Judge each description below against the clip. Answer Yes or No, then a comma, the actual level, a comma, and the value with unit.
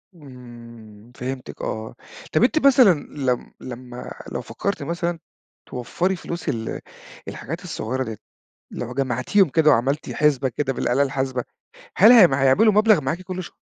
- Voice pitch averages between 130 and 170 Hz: Yes, low, 135 Hz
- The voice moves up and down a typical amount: No, wide, 6.0 semitones